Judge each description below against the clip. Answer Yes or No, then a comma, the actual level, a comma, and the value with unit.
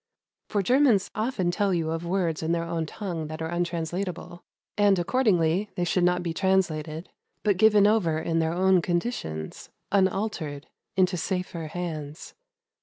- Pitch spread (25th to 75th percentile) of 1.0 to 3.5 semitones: Yes, average, 3.1 semitones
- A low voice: No, medium, 175 Hz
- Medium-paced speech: Yes, average, 150 wpm